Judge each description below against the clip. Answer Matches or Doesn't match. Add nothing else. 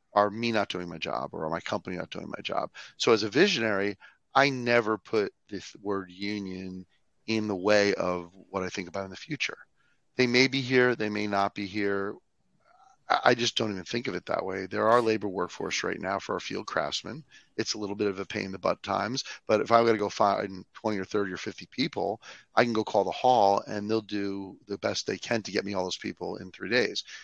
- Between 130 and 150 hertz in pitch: Doesn't match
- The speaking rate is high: Matches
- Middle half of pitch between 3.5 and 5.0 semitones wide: Doesn't match